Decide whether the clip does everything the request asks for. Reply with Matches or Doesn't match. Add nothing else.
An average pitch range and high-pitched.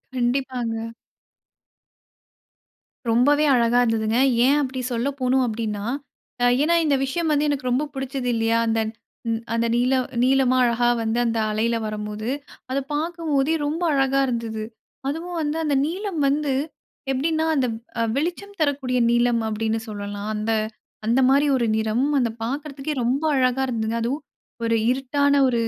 Matches